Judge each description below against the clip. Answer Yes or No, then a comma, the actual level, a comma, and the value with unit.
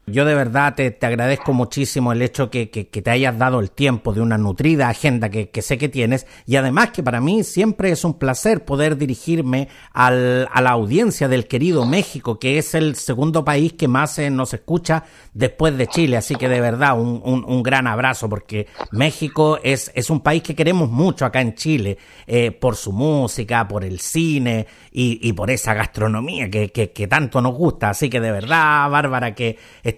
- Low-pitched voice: Yes, low, 130 Hz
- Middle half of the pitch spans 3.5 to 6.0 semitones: Yes, average, 4.1 semitones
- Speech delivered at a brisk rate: Yes, fast, 205 wpm